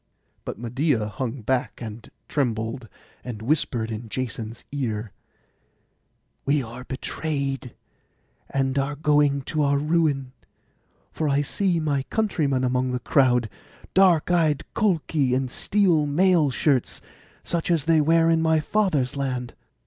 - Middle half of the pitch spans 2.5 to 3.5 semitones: No, average, 3.9 semitones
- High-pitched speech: No, medium, 140 Hz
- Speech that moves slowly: Yes, slow, 130 wpm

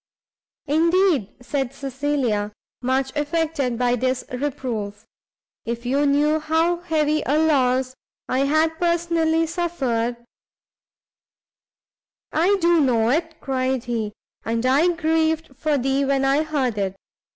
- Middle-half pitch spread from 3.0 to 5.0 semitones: Yes, average, 4.2 semitones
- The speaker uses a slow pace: Yes, slow, 120 wpm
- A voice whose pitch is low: No, very high, 280 Hz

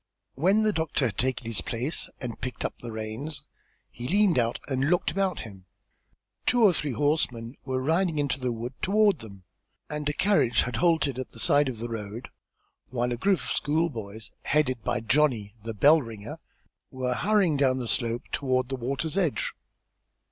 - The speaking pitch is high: No, low, 130 Hz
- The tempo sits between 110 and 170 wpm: No, average, 180 wpm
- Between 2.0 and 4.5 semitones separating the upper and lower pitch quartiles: No, average, 5.1 semitones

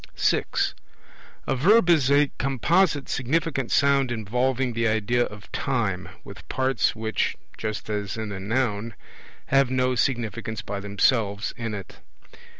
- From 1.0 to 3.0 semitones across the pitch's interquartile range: No, average, 4.0 semitones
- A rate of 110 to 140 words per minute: Yes, slow, 135 wpm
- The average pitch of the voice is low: Yes, low, 120 Hz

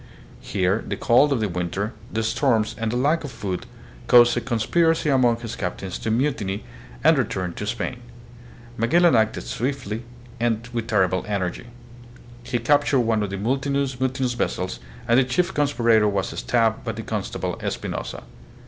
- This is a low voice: Yes, low, 120 Hz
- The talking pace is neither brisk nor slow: Yes, average, 165 wpm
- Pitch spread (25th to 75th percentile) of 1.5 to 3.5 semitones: No, average, 4.2 semitones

